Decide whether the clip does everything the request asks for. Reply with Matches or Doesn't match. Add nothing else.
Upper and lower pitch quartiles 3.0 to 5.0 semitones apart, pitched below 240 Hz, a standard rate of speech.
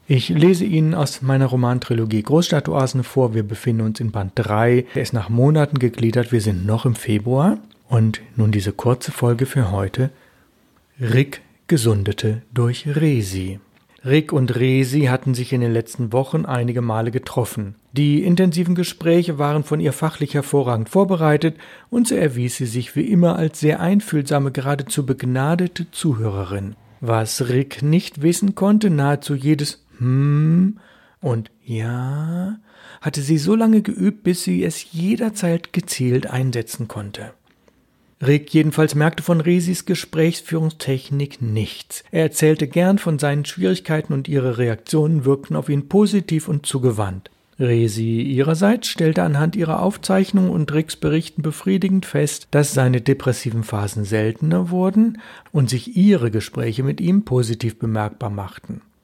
Doesn't match